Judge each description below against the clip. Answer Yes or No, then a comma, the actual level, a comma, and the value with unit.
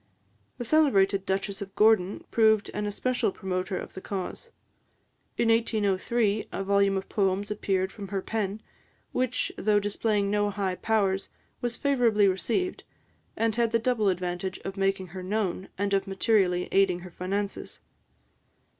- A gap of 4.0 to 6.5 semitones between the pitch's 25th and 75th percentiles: No, narrow, 2.4 semitones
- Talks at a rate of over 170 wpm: No, average, 145 wpm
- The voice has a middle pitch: No, high, 200 Hz